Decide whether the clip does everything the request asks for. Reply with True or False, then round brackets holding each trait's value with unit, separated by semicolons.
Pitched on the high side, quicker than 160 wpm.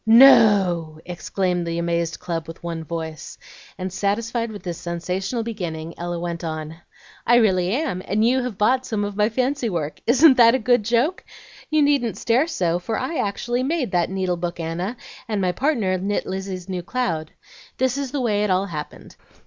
True (195 Hz; 185 wpm)